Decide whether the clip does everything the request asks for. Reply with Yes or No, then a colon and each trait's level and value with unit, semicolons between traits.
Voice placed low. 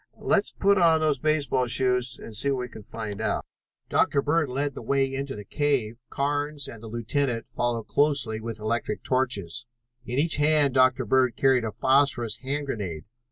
Yes: low, 130 Hz